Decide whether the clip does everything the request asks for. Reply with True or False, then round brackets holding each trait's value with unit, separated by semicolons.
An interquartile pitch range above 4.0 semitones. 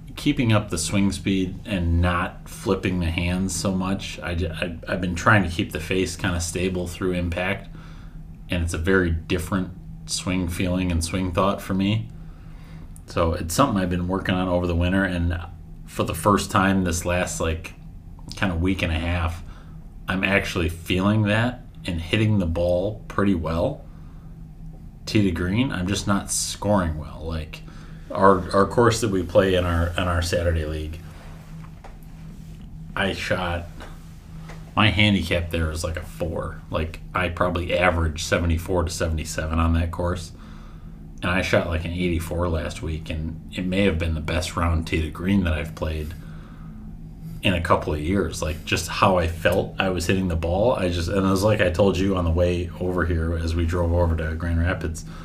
False (2.6 semitones)